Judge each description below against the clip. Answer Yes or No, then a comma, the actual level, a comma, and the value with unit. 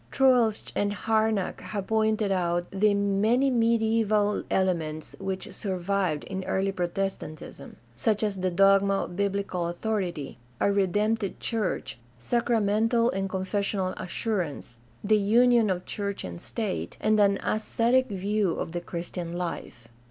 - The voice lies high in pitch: Yes, high, 200 Hz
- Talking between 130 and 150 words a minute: Yes, slow, 135 wpm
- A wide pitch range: No, average, 3.0 semitones